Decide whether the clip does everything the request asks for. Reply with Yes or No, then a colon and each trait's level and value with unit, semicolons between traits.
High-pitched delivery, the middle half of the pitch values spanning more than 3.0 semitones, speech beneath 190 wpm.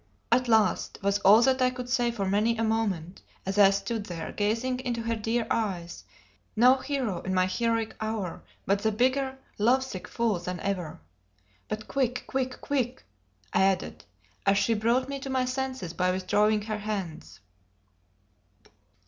Yes: high, 220 Hz; average, 4.2 semitones; average, 165 wpm